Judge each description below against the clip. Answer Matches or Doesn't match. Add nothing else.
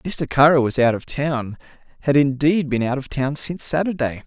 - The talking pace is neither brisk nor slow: Matches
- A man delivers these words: Matches